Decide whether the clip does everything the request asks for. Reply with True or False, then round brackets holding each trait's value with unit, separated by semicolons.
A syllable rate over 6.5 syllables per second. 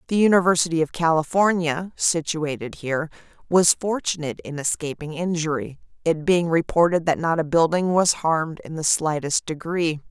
False (5.1 syllables/s)